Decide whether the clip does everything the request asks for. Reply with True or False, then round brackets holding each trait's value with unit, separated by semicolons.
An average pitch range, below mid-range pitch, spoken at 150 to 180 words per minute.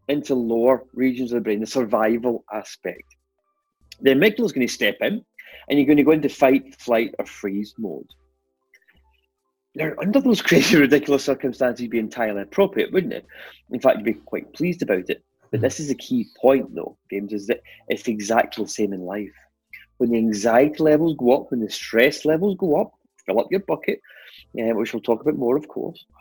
False (5.0 semitones; 125 Hz; 195 wpm)